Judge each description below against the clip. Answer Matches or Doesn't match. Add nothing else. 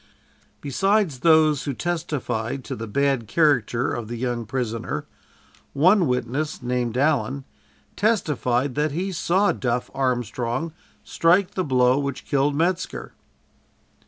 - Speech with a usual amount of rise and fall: Matches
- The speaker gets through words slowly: Matches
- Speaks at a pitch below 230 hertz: Matches